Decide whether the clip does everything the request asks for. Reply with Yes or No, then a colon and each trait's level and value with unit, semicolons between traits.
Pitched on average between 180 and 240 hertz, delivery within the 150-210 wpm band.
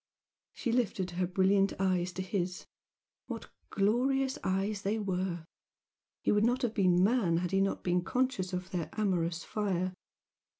Yes: high, 190 Hz; average, 155 wpm